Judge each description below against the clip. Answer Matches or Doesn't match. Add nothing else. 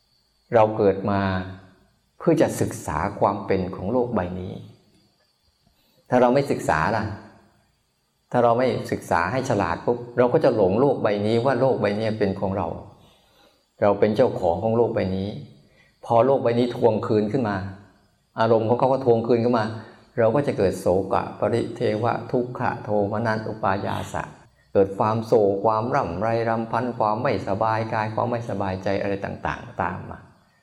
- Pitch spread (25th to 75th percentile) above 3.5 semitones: Doesn't match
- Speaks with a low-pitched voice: Matches